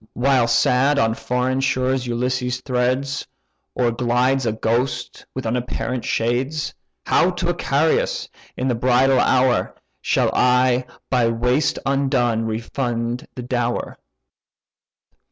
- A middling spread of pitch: No, narrow, 1.7 semitones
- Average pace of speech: No, slow, 115 wpm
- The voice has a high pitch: No, low, 125 Hz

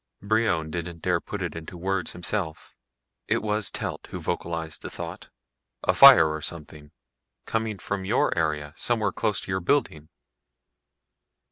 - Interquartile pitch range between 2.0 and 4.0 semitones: No, average, 4.6 semitones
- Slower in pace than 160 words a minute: Yes, average, 145 wpm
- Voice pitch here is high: No, very low, 90 Hz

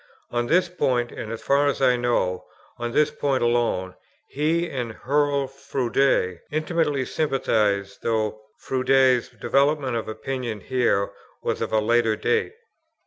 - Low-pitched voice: Yes, low, 130 Hz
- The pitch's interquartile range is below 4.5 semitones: Yes, average, 3.8 semitones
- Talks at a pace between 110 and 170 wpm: Yes, average, 140 wpm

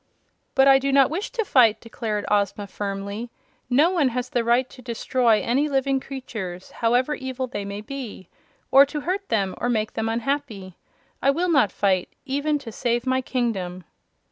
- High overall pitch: Yes, high, 245 Hz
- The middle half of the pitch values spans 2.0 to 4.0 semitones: No, average, 4.4 semitones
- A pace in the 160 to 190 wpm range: Yes, average, 175 wpm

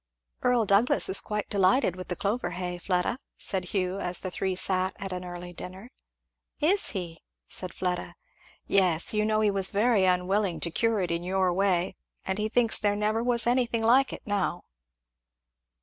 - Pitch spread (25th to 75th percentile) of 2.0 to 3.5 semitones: Yes, average, 3.1 semitones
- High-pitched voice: Yes, high, 195 Hz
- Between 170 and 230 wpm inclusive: Yes, average, 180 wpm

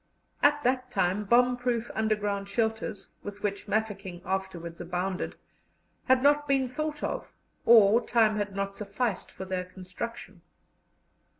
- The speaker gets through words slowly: Yes, slow, 130 wpm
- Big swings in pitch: No, average, 4.1 semitones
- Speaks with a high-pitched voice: Yes, high, 210 Hz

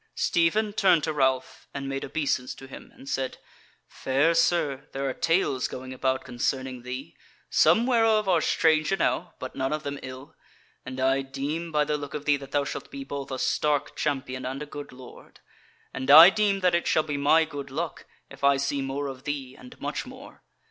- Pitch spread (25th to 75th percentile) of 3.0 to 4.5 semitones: Yes, average, 3.3 semitones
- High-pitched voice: No, medium, 140 Hz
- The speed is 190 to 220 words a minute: Yes, average, 200 wpm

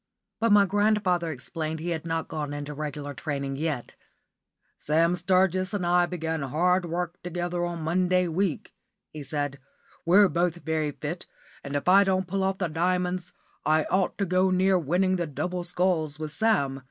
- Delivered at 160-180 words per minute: Yes, average, 170 wpm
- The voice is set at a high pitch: No, medium, 175 Hz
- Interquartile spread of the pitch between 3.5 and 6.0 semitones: No, average, 3.0 semitones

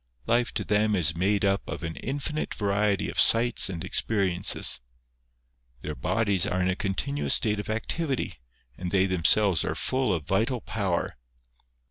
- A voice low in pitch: Yes, low, 100 Hz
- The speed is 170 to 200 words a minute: No, average, 155 wpm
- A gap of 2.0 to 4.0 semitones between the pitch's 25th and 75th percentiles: Yes, average, 3.5 semitones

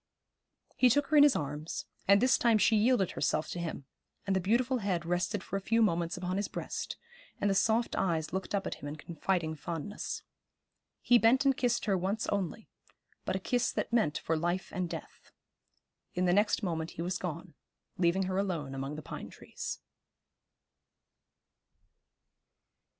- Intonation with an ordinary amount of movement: Yes, average, 4.7 semitones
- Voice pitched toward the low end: No, high, 190 Hz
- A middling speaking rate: Yes, average, 175 wpm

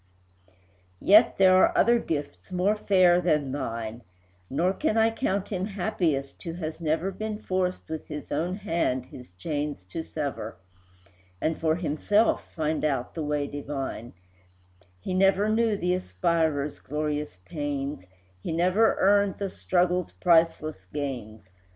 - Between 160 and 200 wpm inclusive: No, average, 140 wpm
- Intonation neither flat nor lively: Yes, average, 4.5 semitones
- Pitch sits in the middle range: Yes, medium, 165 Hz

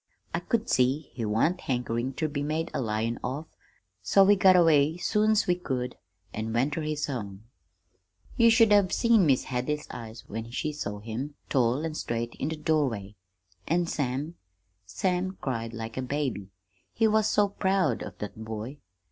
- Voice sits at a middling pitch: Yes, medium, 145 Hz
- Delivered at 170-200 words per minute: Yes, average, 175 wpm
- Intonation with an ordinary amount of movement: No, wide, 7.1 semitones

